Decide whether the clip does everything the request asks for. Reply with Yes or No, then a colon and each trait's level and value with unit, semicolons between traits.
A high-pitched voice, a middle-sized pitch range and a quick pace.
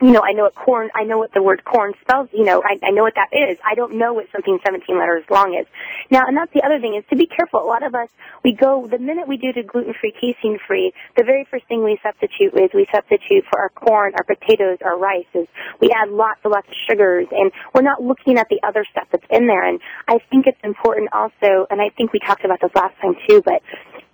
Yes: high, 220 Hz; average, 4.7 semitones; fast, 265 wpm